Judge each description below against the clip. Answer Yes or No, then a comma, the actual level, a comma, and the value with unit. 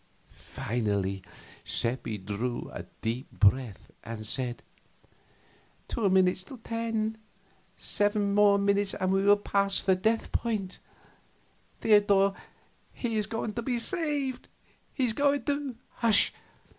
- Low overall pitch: No, high, 200 Hz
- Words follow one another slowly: Yes, slow, 120 wpm